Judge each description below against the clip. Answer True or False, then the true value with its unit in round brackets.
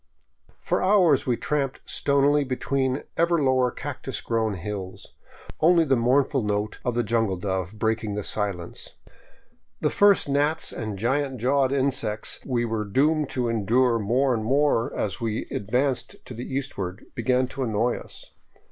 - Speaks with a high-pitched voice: False (125 Hz)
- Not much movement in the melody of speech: False (4.2 semitones)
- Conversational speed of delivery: True (155 wpm)